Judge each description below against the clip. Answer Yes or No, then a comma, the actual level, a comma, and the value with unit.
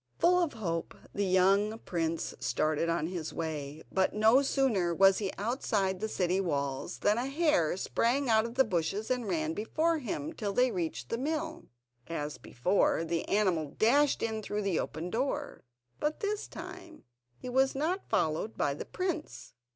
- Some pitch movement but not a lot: No, wide, 8.0 semitones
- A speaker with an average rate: Yes, average, 170 wpm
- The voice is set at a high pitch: Yes, high, 210 Hz